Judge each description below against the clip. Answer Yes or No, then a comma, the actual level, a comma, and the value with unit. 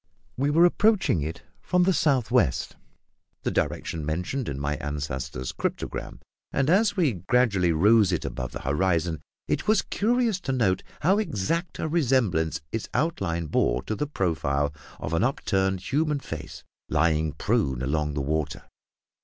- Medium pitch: No, very low, 95 Hz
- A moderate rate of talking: Yes, average, 155 wpm